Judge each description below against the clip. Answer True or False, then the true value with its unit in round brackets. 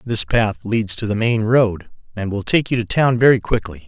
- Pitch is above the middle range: False (110 Hz)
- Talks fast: True (230 wpm)